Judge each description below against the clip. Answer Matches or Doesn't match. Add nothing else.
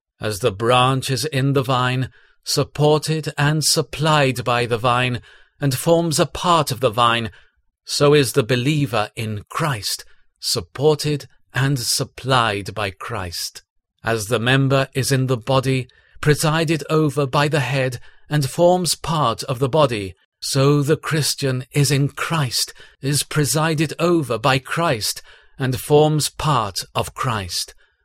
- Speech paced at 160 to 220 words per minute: Doesn't match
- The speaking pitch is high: Doesn't match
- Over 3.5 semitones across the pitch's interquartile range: Doesn't match